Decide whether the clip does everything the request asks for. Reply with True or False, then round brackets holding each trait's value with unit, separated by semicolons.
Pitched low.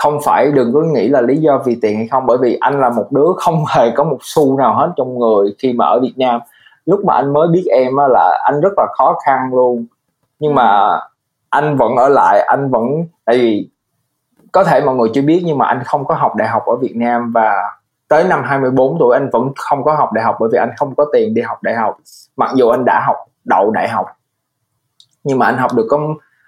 True (130 Hz)